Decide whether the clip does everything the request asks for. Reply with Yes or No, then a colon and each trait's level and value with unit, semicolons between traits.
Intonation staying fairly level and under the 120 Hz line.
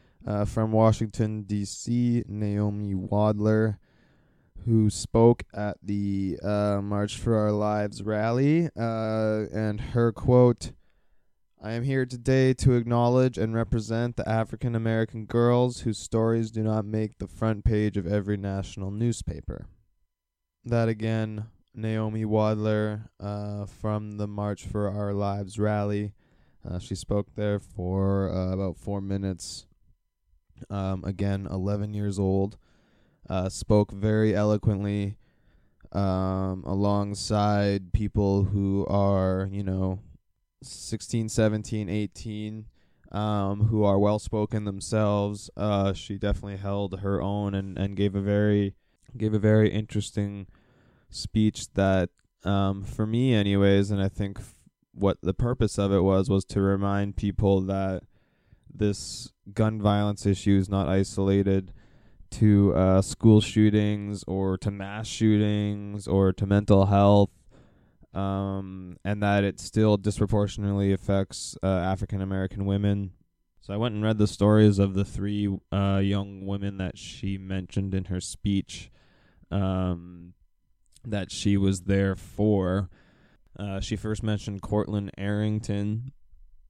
Yes: narrow, 1.7 semitones; low, 100 Hz